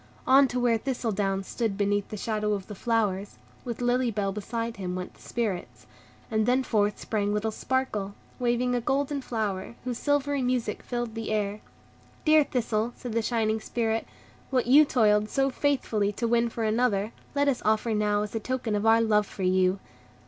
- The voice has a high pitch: Yes, high, 225 Hz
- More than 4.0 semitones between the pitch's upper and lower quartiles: No, average, 3.0 semitones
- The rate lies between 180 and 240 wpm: Yes, average, 185 wpm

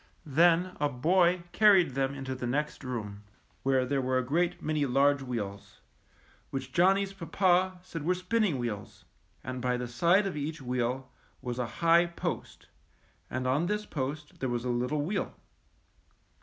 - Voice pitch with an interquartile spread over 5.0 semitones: Yes, wide, 5.5 semitones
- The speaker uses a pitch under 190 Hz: Yes, medium, 140 Hz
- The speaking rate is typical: Yes, average, 160 wpm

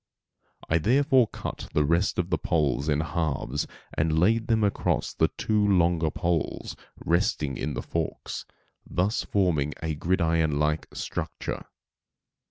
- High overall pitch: No, very low, 85 Hz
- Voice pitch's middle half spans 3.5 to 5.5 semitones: Yes, average, 4.4 semitones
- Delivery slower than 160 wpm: Yes, slow, 135 wpm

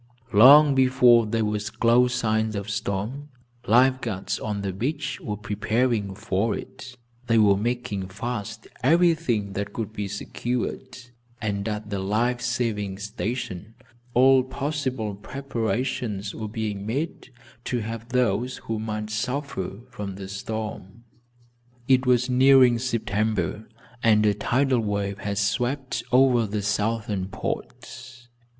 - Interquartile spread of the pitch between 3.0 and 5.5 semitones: Yes, average, 3.4 semitones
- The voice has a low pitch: Yes, low, 110 Hz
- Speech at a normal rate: No, slow, 130 wpm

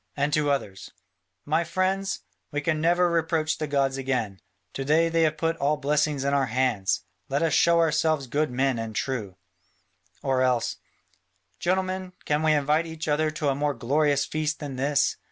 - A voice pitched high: No, medium, 150 Hz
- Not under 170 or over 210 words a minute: Yes, average, 175 wpm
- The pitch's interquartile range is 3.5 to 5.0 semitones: No, average, 3.0 semitones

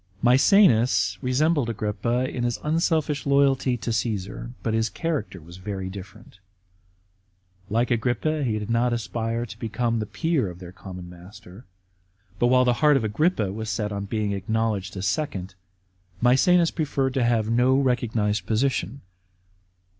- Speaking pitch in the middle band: No, low, 115 Hz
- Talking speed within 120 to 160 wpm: Yes, average, 145 wpm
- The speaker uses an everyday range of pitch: Yes, average, 4.2 semitones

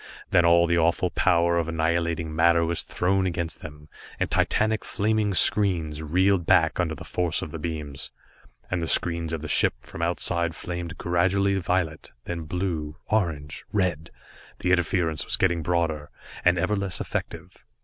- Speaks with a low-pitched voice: Yes, very low, 85 Hz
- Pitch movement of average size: No, narrow, 2.0 semitones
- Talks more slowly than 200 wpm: Yes, average, 160 wpm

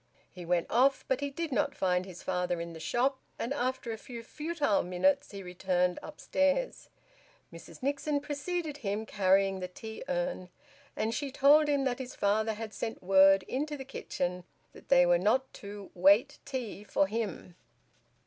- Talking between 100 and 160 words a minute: No, average, 170 wpm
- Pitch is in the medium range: No, high, 225 Hz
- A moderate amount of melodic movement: No, wide, 6.7 semitones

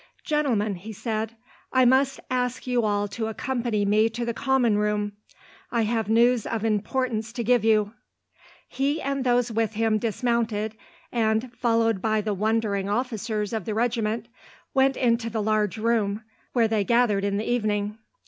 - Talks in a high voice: Yes, high, 225 Hz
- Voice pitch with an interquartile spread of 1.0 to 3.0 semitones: Yes, narrow, 2.4 semitones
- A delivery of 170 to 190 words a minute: No, average, 160 wpm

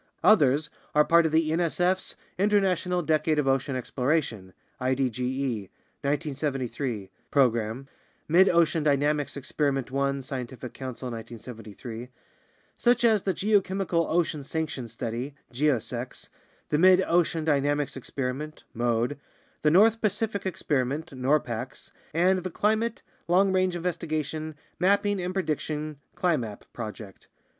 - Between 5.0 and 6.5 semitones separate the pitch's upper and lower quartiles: Yes, wide, 5.5 semitones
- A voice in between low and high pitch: Yes, medium, 150 Hz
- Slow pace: Yes, slow, 115 wpm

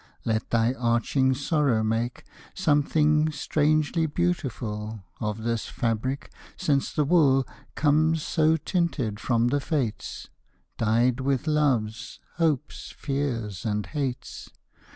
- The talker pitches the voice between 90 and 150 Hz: Yes, low, 135 Hz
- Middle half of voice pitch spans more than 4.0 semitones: Yes, average, 4.9 semitones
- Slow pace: Yes, slow, 110 wpm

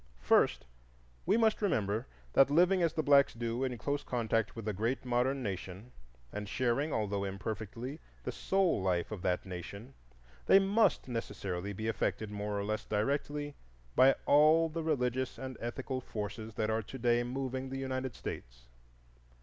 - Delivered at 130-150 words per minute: No, average, 160 wpm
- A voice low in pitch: Yes, low, 120 Hz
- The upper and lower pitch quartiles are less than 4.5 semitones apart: No, average, 5.0 semitones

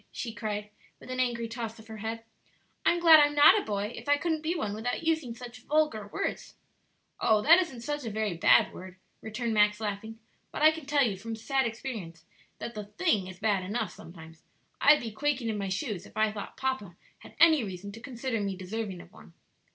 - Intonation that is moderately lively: Yes, average, 4.6 semitones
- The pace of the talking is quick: Yes, fast, 215 wpm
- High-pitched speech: Yes, high, 225 Hz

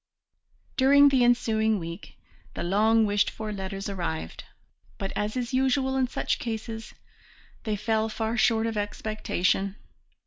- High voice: Yes, high, 220 Hz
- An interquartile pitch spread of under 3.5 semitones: Yes, average, 2.8 semitones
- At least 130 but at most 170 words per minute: Yes, slow, 135 wpm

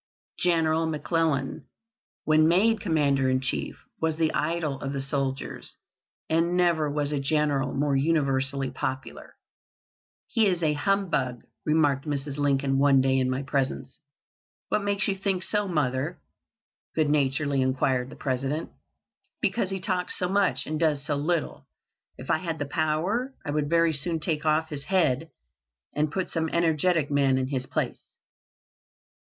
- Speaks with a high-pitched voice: No, medium, 150 Hz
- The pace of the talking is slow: No, average, 150 wpm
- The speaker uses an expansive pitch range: No, average, 3.5 semitones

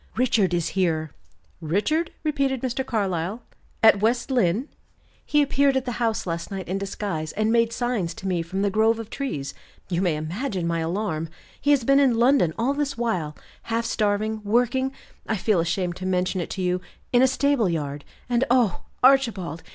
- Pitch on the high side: Yes, high, 215 Hz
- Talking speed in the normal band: Yes, average, 180 wpm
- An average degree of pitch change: No, wide, 6.0 semitones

